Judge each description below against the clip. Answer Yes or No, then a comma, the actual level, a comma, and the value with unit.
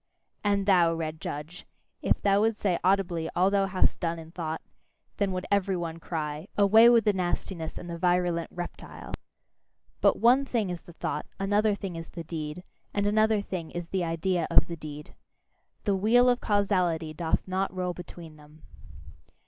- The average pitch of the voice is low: No, medium, 180 Hz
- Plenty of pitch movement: No, average, 3.4 semitones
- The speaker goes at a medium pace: Yes, average, 175 wpm